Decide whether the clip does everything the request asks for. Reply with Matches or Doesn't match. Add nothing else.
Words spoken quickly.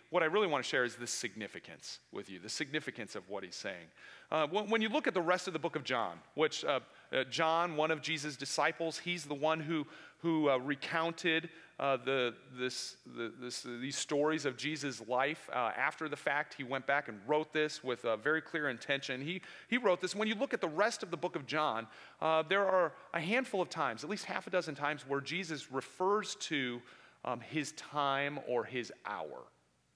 Matches